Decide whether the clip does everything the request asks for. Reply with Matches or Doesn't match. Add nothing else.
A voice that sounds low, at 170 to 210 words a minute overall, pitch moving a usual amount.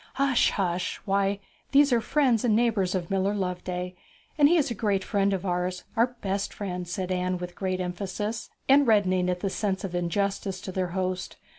Doesn't match